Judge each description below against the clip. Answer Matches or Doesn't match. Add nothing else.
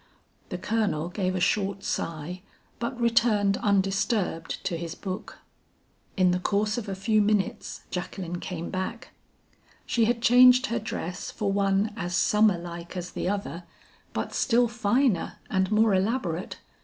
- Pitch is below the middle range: Doesn't match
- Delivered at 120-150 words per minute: Matches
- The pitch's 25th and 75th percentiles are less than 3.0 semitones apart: Doesn't match